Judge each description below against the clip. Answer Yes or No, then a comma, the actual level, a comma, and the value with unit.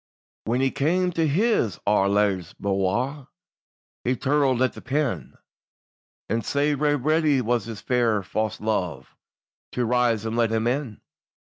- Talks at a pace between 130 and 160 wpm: Yes, average, 140 wpm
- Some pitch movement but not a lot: Yes, average, 4.7 semitones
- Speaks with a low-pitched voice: Yes, low, 120 Hz